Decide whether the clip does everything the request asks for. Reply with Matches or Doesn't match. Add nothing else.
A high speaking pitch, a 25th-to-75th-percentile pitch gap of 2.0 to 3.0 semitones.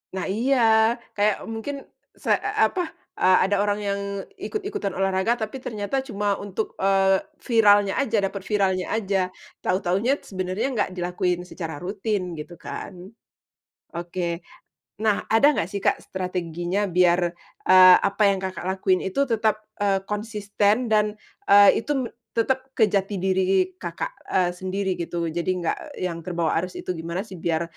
Matches